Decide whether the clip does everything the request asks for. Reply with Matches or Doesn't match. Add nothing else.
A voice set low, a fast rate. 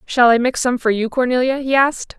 Doesn't match